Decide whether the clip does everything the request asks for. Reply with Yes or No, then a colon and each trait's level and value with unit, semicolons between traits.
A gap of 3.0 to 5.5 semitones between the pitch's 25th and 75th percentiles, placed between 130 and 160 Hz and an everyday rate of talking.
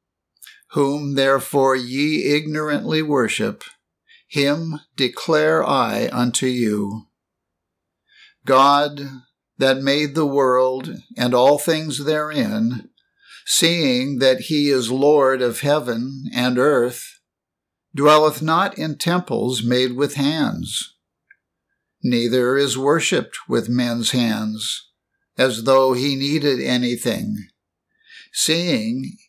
No: average, 3.5 semitones; medium, 140 Hz; slow, 95 wpm